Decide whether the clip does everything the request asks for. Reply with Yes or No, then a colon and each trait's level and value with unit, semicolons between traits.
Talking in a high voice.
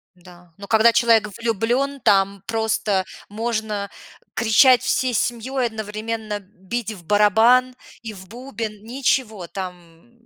Yes: high, 220 Hz